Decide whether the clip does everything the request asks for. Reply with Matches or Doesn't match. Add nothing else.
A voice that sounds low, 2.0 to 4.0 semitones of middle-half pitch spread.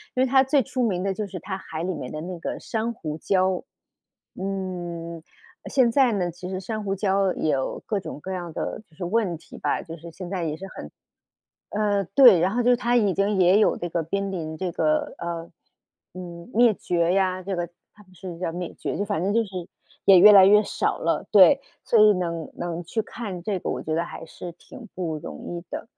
Doesn't match